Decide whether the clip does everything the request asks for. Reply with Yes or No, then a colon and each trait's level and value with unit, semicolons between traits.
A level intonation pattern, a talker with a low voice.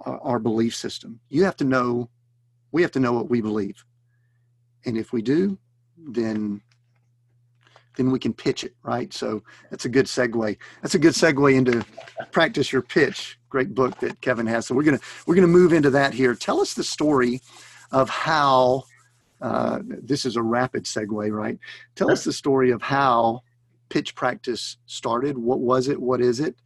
Yes: narrow, 1.7 semitones; low, 120 Hz